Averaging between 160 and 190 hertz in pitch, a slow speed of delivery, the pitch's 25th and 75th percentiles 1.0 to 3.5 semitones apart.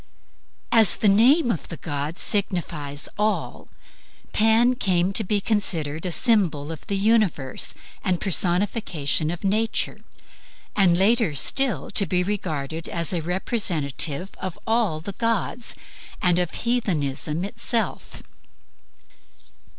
No: medium, 185 Hz; slow, 120 wpm; average, 5.2 semitones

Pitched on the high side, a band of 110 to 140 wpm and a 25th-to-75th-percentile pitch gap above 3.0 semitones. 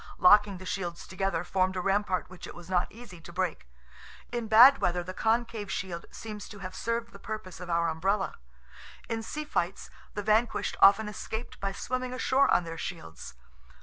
No: high, 195 Hz; average, 180 wpm; average, 3.7 semitones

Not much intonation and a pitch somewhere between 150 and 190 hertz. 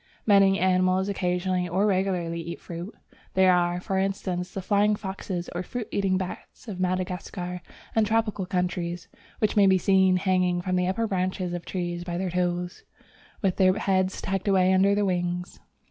Yes: narrow, 1.5 semitones; medium, 185 Hz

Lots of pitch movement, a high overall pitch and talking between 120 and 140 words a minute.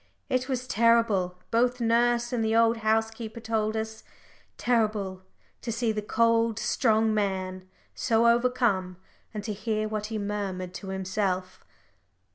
No: narrow, 2.4 semitones; high, 220 Hz; slow, 135 wpm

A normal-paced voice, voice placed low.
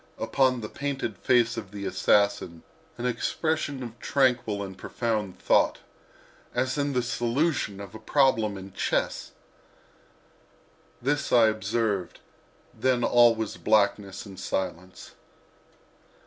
No: slow, 120 wpm; low, 115 Hz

